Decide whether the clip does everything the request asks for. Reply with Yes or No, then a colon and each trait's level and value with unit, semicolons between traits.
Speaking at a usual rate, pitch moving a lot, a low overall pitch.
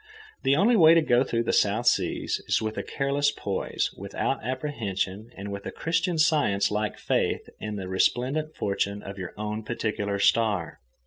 Yes: average, 180 wpm; wide, 6.2 semitones; low, 110 Hz